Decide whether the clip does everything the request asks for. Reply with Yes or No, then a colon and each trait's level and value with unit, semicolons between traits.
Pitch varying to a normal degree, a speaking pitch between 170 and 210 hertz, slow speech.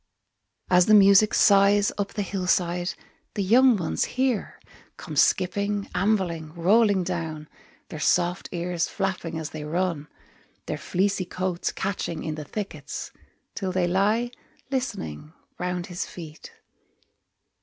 Yes: average, 3.0 semitones; medium, 185 Hz; slow, 130 wpm